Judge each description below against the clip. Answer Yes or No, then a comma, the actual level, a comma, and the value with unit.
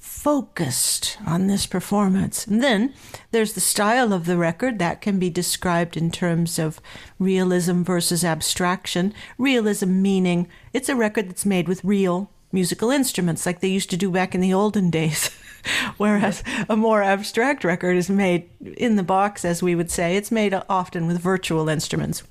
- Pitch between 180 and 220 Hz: Yes, high, 190 Hz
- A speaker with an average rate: Yes, average, 170 wpm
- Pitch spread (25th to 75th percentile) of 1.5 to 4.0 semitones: Yes, average, 2.8 semitones